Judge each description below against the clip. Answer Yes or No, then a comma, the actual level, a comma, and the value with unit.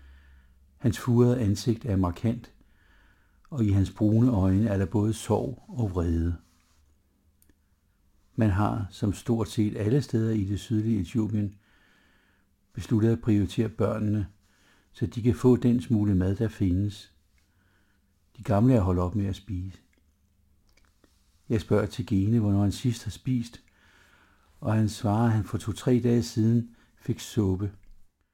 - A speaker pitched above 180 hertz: No, low, 105 Hz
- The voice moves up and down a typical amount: Yes, average, 3.5 semitones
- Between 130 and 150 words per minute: Yes, slow, 145 wpm